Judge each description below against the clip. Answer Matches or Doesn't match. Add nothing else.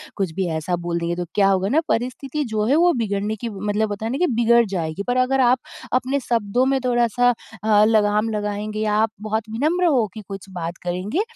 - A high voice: Matches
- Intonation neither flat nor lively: Matches